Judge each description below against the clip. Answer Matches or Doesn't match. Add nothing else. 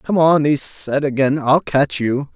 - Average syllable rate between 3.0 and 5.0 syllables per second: Matches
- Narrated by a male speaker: Matches